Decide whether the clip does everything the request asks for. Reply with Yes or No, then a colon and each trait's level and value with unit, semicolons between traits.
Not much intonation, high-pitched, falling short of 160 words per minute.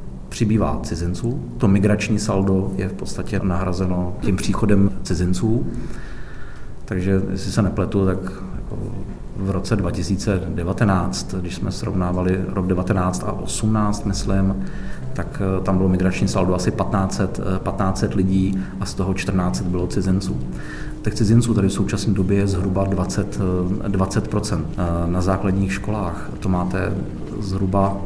No: narrow, 1.3 semitones; very low, 95 Hz; average, 125 wpm